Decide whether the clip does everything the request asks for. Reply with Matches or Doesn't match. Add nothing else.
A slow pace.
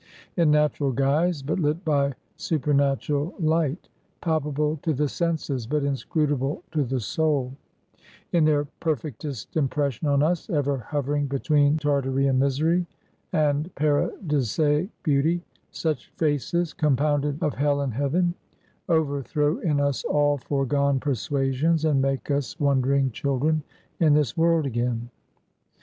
Matches